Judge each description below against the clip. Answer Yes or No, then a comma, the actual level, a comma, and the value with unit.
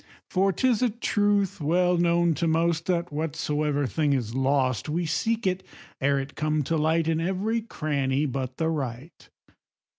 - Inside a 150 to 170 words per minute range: Yes, average, 160 wpm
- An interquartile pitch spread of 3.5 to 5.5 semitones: Yes, average, 4.0 semitones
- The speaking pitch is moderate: Yes, medium, 160 Hz